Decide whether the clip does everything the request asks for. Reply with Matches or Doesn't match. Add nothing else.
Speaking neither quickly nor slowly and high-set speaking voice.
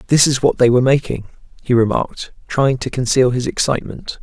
Doesn't match